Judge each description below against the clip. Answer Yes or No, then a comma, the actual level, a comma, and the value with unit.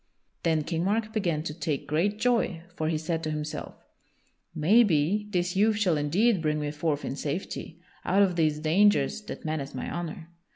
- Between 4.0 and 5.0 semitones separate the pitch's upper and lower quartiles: Yes, average, 4.6 semitones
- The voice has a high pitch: No, medium, 165 Hz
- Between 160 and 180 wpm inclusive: Yes, average, 175 wpm